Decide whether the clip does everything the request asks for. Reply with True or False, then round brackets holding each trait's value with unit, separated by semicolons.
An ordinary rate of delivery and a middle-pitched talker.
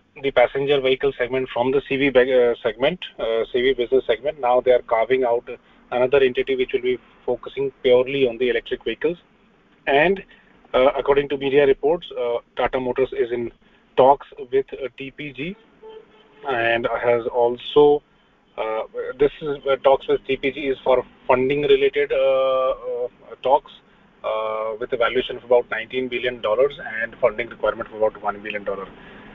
True (160 wpm; 180 Hz)